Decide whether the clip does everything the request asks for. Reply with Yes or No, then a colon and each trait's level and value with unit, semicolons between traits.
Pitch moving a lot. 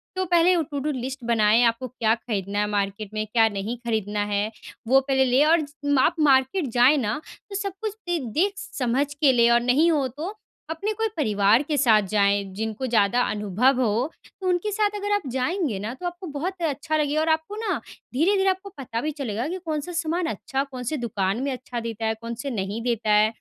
Yes: wide, 6.5 semitones